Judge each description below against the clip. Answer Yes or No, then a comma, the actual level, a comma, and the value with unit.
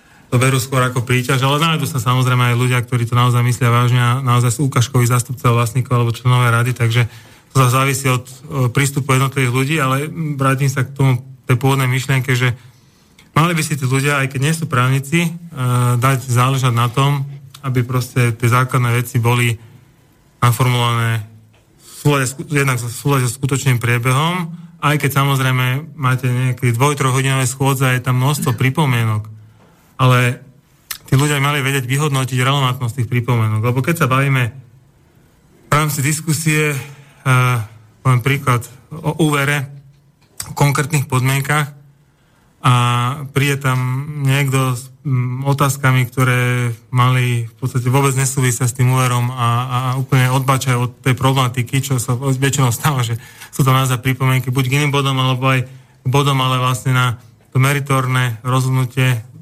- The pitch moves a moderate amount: No, narrow, 2.0 semitones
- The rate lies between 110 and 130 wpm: No, average, 155 wpm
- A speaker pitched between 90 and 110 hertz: No, low, 130 Hz